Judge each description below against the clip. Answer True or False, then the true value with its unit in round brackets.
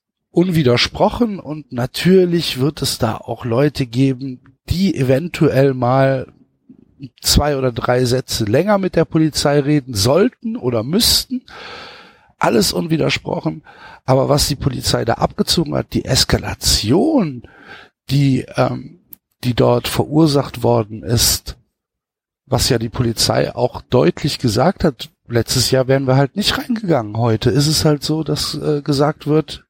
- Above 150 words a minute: False (135 wpm)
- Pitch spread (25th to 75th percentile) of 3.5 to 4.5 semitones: True (4.2 semitones)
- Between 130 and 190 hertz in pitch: True (140 Hz)